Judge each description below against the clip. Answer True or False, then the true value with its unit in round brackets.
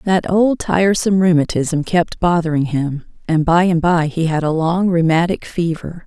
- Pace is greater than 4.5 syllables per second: True (4.7 syllables/s)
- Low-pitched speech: False (170 Hz)